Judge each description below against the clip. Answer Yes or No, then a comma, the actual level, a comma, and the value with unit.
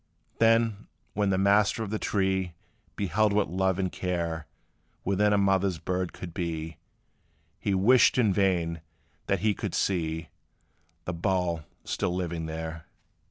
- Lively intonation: No, average, 3.2 semitones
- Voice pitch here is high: No, very low, 95 Hz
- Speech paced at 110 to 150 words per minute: Yes, average, 140 wpm